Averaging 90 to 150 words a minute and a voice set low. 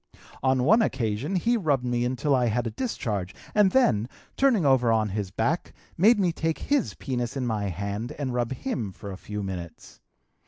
No: average, 190 wpm; low, 125 Hz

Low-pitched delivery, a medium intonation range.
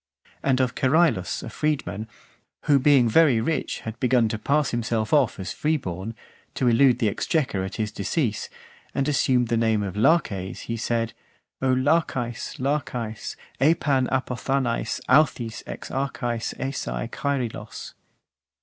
Yes: low, 125 Hz; average, 3.8 semitones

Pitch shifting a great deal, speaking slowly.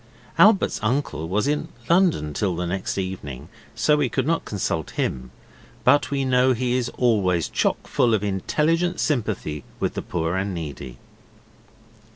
No: wide, 8.0 semitones; average, 155 wpm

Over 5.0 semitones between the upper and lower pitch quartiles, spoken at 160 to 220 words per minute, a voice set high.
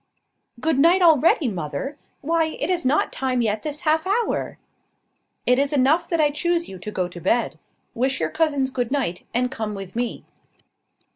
Yes: wide, 5.4 semitones; average, 175 wpm; very high, 275 Hz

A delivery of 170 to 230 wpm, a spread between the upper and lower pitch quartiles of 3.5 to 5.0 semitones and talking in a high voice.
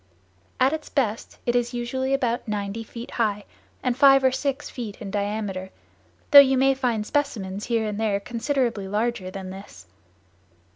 No: average, 160 wpm; average, 4.2 semitones; high, 230 Hz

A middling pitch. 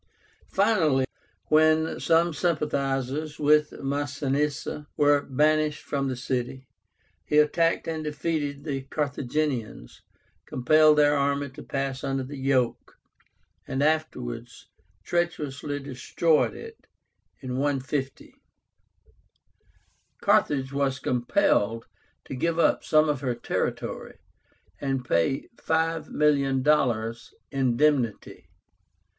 Yes: medium, 145 Hz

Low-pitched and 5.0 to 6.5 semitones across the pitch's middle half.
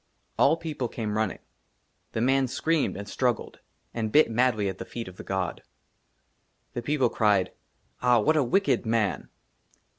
No: low, 120 Hz; average, 4.2 semitones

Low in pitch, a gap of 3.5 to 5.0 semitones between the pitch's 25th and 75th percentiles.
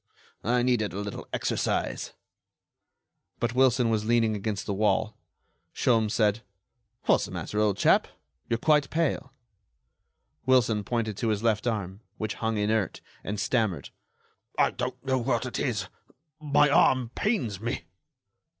No: low, 110 Hz; average, 3.0 semitones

